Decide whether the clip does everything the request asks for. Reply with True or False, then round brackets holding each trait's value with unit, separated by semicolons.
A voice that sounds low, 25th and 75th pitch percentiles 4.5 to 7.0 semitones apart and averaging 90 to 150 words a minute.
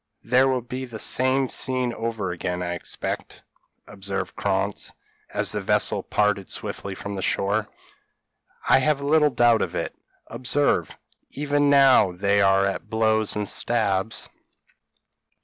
True (110 Hz; 4.8 semitones; 140 wpm)